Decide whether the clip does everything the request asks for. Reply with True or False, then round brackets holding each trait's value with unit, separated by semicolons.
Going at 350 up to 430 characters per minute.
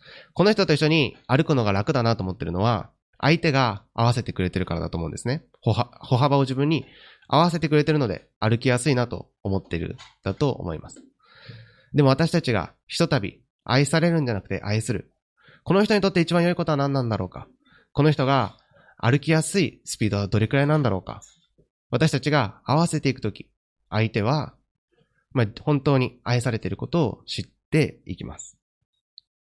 True (370 characters per minute)